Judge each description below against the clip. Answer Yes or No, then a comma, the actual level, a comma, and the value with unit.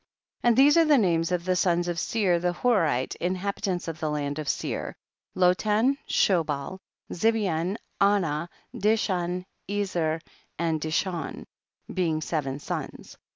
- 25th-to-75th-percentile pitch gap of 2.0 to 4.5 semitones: Yes, average, 3.9 semitones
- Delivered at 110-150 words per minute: Yes, average, 140 wpm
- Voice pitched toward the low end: No, medium, 175 Hz